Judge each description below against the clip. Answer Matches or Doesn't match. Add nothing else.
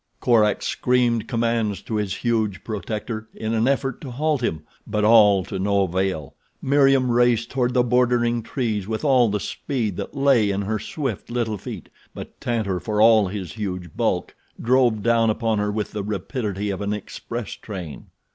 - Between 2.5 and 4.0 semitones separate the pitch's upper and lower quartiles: Matches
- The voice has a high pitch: Doesn't match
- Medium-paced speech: Matches